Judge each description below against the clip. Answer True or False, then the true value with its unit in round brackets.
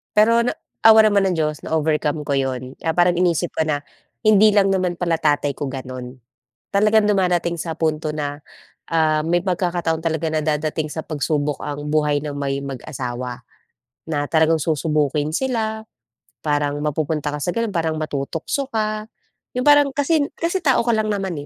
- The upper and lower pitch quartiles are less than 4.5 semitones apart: False (4.8 semitones)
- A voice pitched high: False (160 Hz)